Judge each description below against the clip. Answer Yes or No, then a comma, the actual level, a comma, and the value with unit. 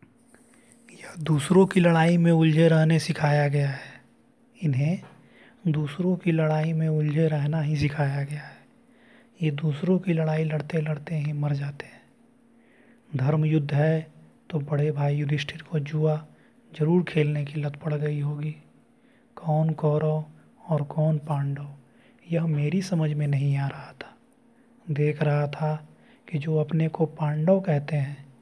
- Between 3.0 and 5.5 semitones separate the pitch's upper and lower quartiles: No, narrow, 2.4 semitones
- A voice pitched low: No, medium, 155 Hz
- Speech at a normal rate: Yes, average, 145 wpm